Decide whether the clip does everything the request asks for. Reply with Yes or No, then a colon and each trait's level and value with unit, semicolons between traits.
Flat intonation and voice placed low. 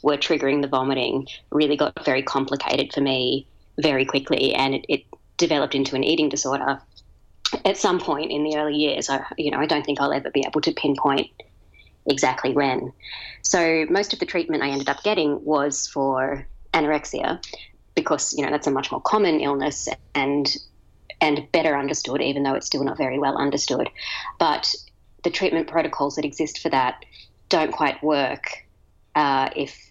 No: narrow, 1.7 semitones; medium, 145 Hz